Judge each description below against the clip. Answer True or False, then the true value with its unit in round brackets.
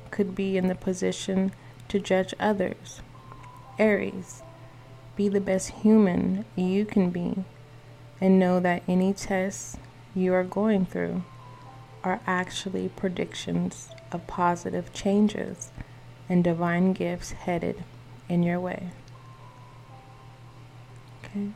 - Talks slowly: True (110 wpm)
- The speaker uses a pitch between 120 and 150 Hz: False (175 Hz)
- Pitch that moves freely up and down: True (6.9 semitones)